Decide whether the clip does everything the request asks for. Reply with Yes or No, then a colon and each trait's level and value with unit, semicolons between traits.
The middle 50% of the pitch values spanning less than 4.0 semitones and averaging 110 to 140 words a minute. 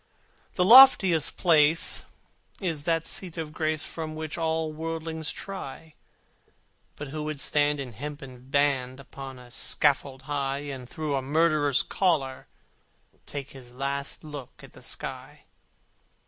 Yes: average, 2.9 semitones; slow, 135 wpm